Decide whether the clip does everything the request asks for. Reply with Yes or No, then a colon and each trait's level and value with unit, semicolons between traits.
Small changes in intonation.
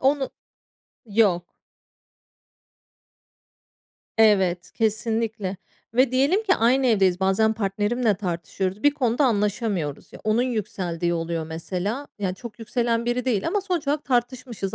No: average, 4.7 semitones